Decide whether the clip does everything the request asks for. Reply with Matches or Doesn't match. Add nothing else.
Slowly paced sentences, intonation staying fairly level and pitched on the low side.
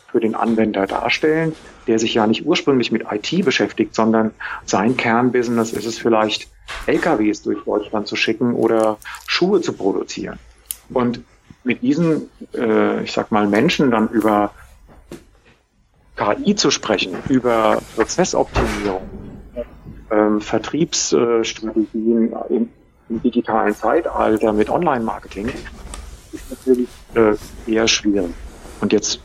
Matches